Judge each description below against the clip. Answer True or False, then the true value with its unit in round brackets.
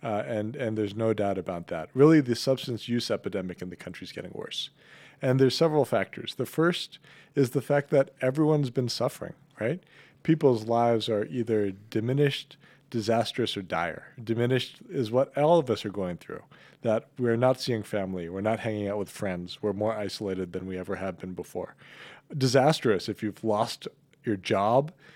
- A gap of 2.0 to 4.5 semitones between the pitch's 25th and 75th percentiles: False (4.9 semitones)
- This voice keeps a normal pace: True (180 wpm)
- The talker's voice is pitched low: True (115 Hz)